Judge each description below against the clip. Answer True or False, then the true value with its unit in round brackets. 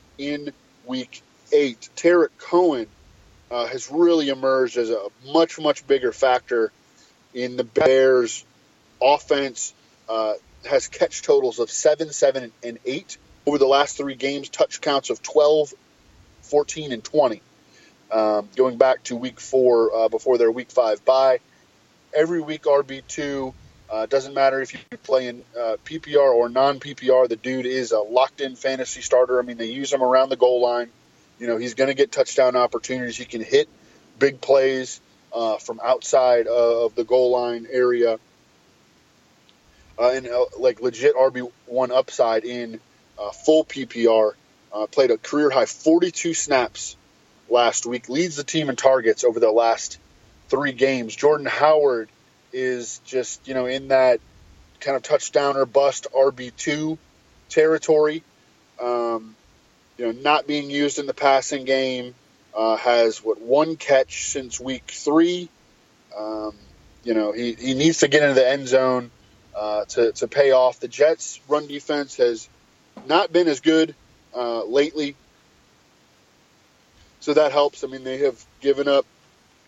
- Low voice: True (130 Hz)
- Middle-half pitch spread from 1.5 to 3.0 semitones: False (3.5 semitones)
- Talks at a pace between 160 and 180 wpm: False (150 wpm)